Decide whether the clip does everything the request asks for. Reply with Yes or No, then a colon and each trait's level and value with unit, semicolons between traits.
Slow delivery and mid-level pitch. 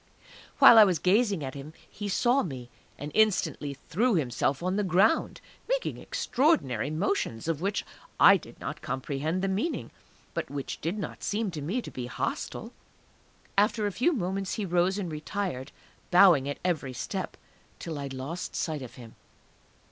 No: average, 165 wpm; medium, 175 Hz